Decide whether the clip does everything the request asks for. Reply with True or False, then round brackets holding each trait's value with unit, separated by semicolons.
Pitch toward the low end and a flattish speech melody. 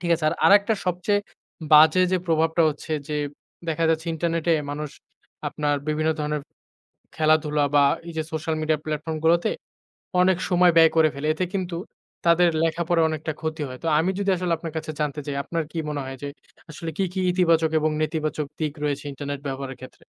False (160 Hz; 1.9 semitones)